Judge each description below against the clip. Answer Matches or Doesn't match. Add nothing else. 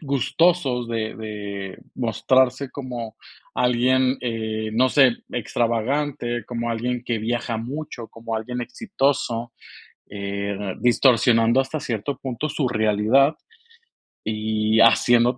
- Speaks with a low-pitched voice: Matches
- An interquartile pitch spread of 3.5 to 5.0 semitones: Doesn't match